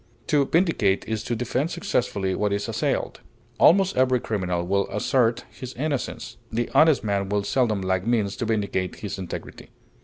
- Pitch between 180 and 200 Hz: No, low, 110 Hz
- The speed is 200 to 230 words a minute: No, average, 160 wpm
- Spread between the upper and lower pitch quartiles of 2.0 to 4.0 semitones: No, average, 4.5 semitones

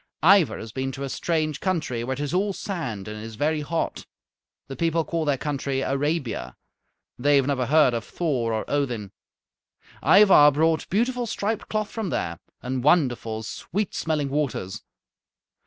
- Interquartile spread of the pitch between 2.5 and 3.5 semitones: No, average, 5.0 semitones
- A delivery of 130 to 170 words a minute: Yes, average, 160 wpm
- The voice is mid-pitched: Yes, medium, 145 Hz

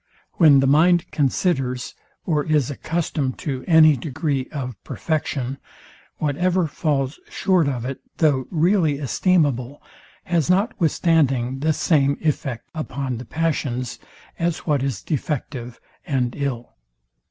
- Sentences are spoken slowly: Yes, slow, 120 wpm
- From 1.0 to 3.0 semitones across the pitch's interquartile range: No, average, 3.6 semitones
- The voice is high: No, medium, 145 Hz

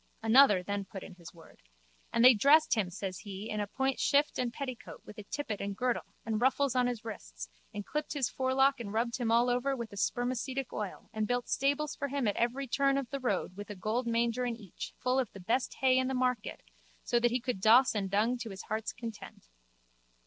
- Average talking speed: No, fast, 225 wpm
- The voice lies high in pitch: Yes, high, 235 Hz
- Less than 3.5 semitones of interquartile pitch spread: No, average, 3.8 semitones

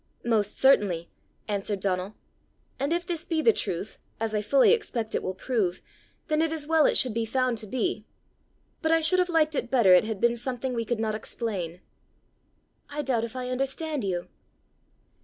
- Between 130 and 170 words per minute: No, average, 185 wpm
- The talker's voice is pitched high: Yes, high, 235 Hz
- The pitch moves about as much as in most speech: No, wide, 5.8 semitones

